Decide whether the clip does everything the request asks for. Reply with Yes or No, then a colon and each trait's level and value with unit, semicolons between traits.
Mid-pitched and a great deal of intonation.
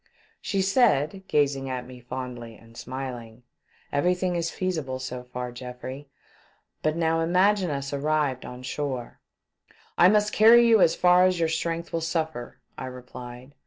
Yes: medium, 145 Hz; wide, 5.7 semitones